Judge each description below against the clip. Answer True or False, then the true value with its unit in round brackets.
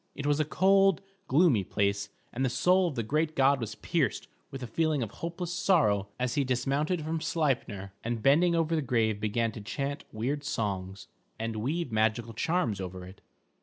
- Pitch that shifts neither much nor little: False (6.4 semitones)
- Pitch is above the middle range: False (130 Hz)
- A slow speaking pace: False (185 wpm)